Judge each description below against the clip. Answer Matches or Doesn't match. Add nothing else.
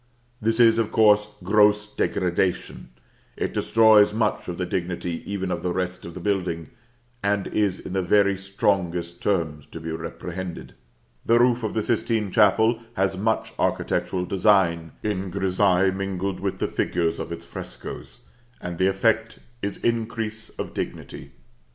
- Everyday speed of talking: Matches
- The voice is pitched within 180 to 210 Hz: Doesn't match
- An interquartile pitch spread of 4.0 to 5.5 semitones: Doesn't match